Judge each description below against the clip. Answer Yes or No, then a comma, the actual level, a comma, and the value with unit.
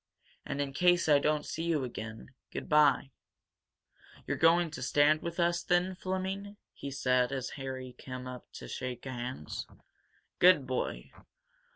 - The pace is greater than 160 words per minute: No, average, 150 wpm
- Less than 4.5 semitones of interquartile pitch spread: No, average, 5.1 semitones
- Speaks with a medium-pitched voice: Yes, medium, 145 Hz